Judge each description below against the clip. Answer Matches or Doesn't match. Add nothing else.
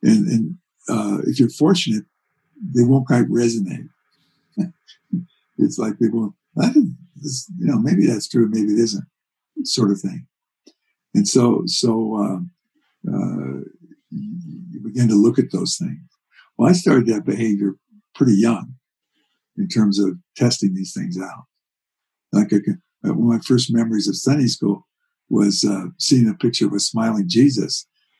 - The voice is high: Doesn't match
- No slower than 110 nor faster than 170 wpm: Matches